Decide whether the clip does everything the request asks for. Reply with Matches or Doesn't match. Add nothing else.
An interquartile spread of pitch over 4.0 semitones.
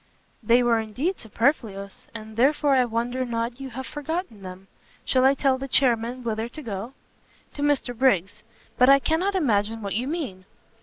Doesn't match